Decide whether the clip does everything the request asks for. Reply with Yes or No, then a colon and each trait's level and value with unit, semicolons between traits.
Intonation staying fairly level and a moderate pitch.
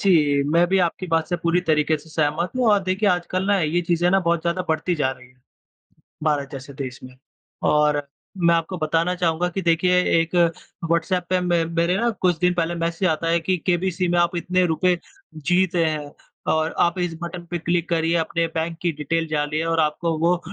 Yes: narrow, 2.0 semitones; medium, 170 Hz